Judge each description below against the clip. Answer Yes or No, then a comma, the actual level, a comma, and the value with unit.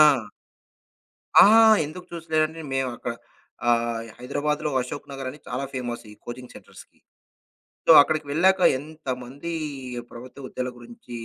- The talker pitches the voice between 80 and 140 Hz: Yes, low, 135 Hz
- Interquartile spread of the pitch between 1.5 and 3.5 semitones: No, average, 4.0 semitones